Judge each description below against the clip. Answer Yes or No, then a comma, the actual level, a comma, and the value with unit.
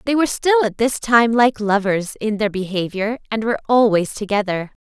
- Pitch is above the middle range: Yes, high, 220 Hz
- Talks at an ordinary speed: Yes, average, 185 wpm